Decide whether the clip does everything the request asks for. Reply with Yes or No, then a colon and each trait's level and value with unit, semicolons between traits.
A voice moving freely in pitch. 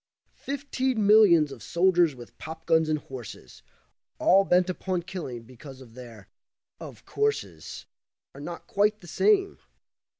Yes: wide, 7.3 semitones